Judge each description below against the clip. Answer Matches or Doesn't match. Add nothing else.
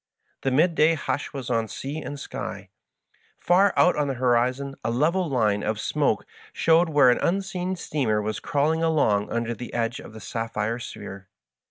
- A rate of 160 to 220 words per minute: Matches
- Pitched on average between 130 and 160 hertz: Matches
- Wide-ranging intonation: Matches